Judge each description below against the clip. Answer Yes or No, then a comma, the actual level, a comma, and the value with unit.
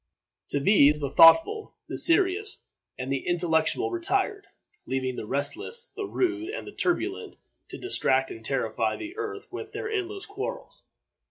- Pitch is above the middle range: Yes, very high, 340 Hz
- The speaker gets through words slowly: No, average, 150 wpm